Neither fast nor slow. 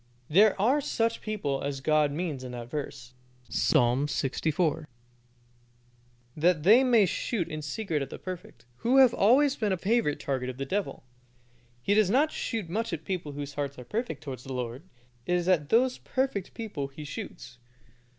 Yes: average, 180 wpm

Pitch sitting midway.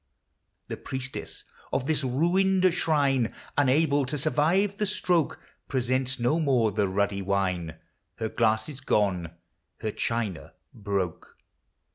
No: low, 130 Hz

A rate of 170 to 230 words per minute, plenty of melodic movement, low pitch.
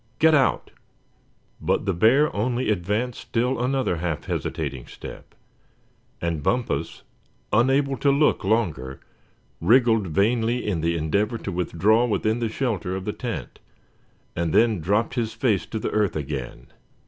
No: average, 140 wpm; wide, 6.1 semitones; low, 110 Hz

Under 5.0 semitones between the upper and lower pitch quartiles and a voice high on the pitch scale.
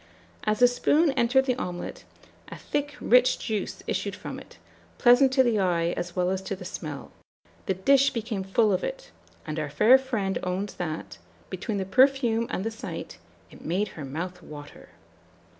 No: wide, 5.6 semitones; high, 205 Hz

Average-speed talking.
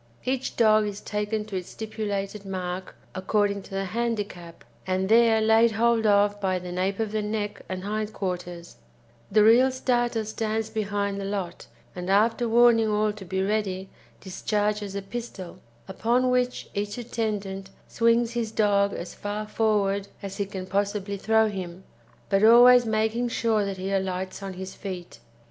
Yes: average, 160 wpm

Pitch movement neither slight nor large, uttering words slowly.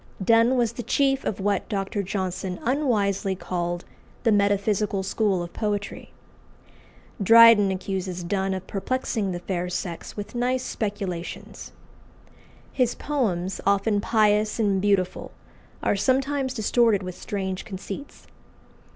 Yes: average, 3.3 semitones; slow, 120 wpm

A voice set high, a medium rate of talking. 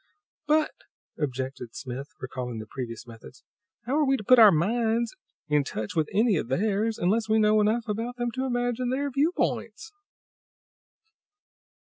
Yes: high, 215 Hz; average, 150 wpm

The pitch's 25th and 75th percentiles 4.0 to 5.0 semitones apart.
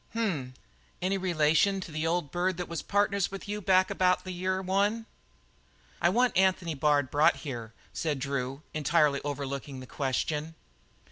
Yes: average, 4.7 semitones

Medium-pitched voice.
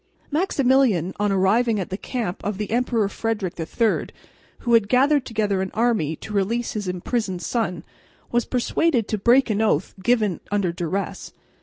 No: high, 215 Hz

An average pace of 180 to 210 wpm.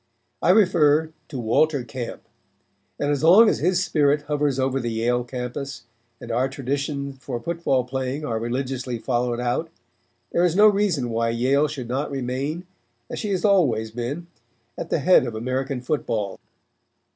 No: average, 160 wpm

